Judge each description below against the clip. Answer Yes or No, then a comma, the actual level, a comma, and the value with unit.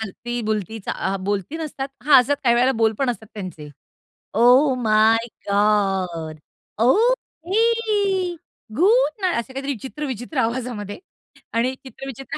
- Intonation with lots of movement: Yes, wide, 5.9 semitones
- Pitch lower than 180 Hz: No, high, 245 Hz